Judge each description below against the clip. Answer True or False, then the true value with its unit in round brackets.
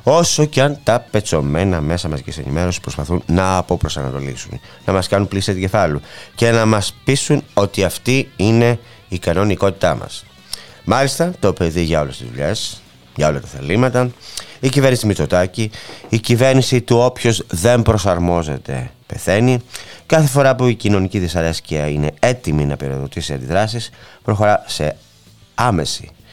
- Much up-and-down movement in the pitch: True (6.2 semitones)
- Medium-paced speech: True (145 wpm)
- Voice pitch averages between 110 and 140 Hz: False (100 Hz)